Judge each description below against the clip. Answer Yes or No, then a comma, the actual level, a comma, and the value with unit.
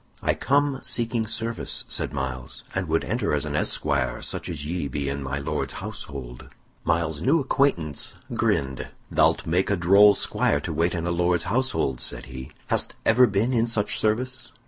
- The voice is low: Yes, very low, 85 Hz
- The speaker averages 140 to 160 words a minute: No, average, 175 wpm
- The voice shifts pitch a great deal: Yes, wide, 8.1 semitones